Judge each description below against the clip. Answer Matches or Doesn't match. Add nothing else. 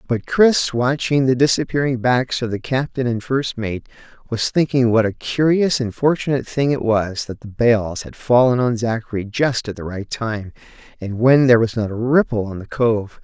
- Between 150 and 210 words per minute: Matches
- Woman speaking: Doesn't match